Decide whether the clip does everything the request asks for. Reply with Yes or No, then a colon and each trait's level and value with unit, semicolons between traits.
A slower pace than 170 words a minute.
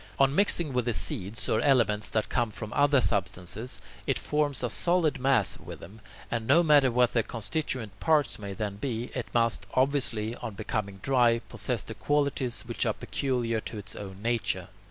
No: average, 180 wpm